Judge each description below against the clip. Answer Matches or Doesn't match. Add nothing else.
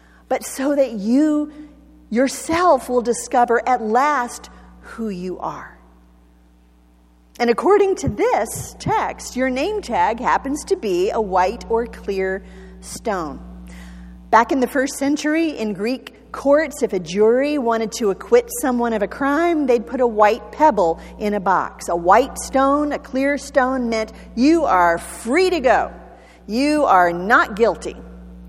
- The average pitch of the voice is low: Doesn't match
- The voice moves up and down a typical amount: Doesn't match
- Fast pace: Doesn't match